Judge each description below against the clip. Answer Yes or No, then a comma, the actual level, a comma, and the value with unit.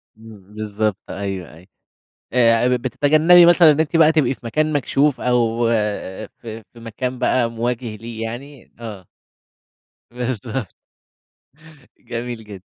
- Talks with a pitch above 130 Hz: No, low, 120 Hz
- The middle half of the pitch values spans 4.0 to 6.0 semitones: No, average, 3.6 semitones